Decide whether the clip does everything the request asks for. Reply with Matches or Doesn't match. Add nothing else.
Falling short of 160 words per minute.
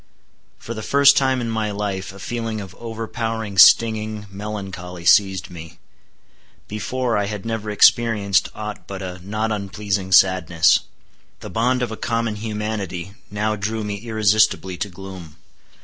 Matches